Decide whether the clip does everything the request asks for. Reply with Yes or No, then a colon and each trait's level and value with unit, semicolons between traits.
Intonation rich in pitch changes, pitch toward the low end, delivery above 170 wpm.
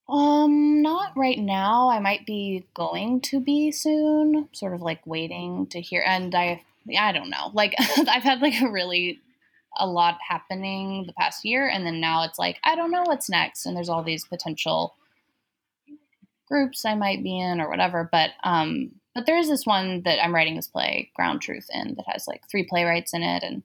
No: wide, 8.4 semitones; high, 200 Hz; average, 200 wpm